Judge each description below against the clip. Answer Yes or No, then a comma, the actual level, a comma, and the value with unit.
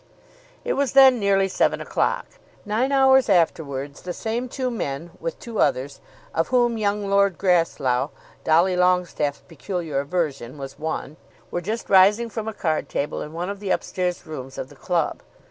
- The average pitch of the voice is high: No, medium, 180 Hz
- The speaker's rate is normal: Yes, average, 170 wpm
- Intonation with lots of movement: Yes, wide, 5.7 semitones